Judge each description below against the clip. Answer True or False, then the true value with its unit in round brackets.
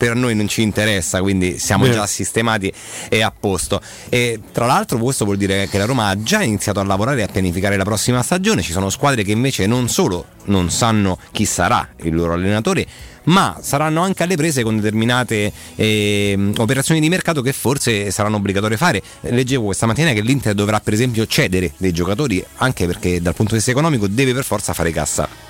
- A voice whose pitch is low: True (105 Hz)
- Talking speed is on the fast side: True (200 wpm)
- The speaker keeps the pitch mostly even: False (4.1 semitones)